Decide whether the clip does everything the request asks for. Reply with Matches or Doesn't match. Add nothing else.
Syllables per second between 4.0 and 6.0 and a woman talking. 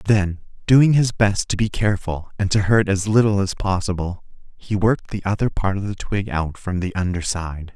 Doesn't match